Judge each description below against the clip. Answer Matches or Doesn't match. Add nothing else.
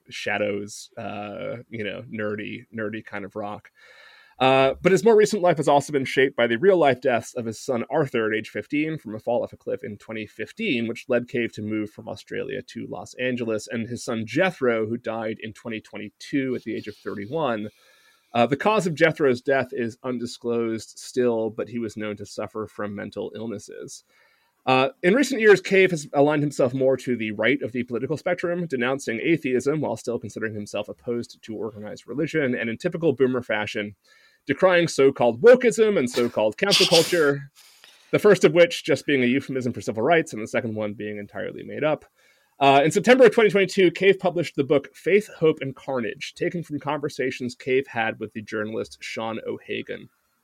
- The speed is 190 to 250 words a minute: Matches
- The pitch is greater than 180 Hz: Doesn't match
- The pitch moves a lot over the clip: Matches